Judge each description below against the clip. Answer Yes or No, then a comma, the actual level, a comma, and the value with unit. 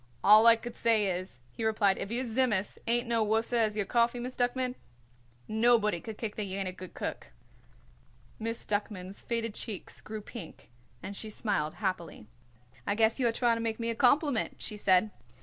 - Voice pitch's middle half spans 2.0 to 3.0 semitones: Yes, narrow, 2.4 semitones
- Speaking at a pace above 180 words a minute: Yes, average, 190 wpm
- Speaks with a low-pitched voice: No, high, 220 Hz